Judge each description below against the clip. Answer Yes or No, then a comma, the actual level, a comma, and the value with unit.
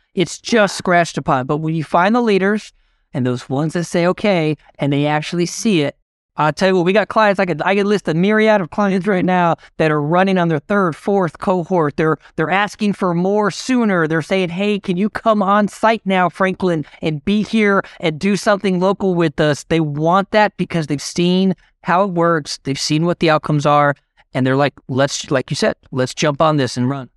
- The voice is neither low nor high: Yes, medium, 175 Hz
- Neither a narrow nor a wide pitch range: Yes, average, 4.5 semitones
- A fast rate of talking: Yes, fast, 220 wpm